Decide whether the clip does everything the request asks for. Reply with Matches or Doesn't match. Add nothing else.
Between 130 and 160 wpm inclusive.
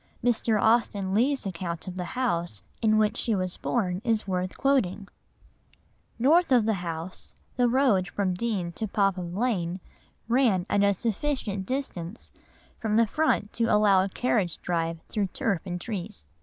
Matches